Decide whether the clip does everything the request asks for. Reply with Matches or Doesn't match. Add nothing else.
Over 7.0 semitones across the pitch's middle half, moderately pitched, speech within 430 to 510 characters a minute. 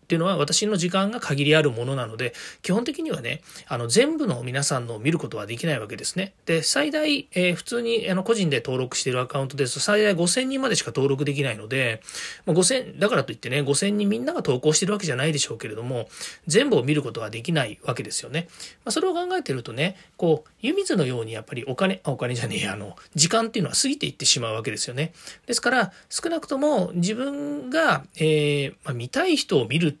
Matches